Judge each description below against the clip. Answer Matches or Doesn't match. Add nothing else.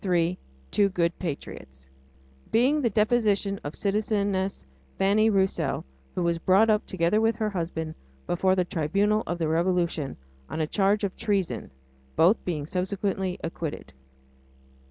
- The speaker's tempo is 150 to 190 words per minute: Doesn't match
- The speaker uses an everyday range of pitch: Matches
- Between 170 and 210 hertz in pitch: Matches